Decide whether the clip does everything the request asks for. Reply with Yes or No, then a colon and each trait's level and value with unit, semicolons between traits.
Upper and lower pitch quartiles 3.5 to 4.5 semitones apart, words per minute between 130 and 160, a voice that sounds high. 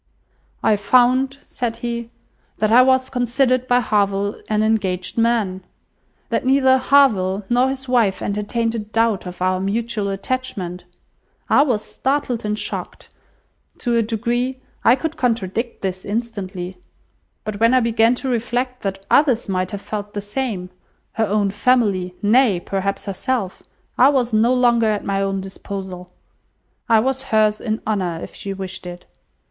Yes: average, 4.1 semitones; average, 150 wpm; high, 220 Hz